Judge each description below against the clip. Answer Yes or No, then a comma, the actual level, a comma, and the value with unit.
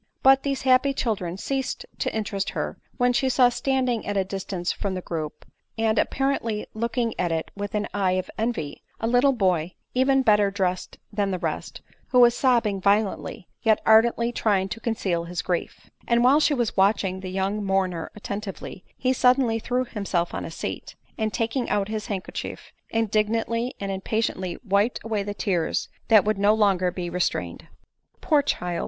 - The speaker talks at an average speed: Yes, average, 180 wpm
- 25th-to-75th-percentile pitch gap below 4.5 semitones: Yes, average, 4.0 semitones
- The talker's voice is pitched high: Yes, high, 210 Hz